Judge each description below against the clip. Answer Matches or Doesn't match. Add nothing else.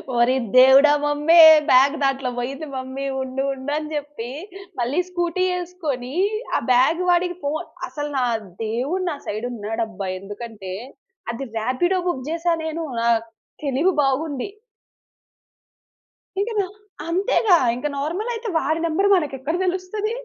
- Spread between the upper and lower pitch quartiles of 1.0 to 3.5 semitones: Doesn't match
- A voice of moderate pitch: Doesn't match